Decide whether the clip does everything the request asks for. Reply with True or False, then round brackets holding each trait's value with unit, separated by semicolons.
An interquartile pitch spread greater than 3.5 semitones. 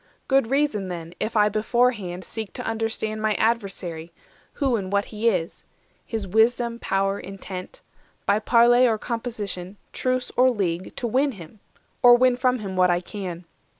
True (4.1 semitones)